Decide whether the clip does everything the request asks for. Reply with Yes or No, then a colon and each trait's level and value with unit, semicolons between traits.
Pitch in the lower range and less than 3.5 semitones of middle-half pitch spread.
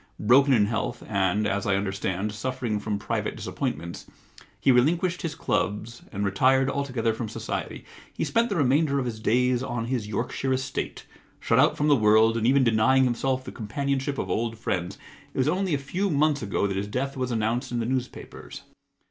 No: low, 120 Hz; average, 4.0 semitones